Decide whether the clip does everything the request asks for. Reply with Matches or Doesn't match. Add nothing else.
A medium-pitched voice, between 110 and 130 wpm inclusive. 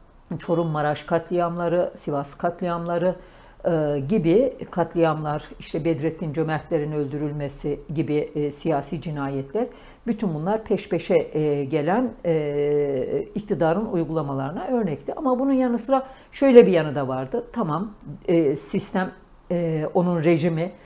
Matches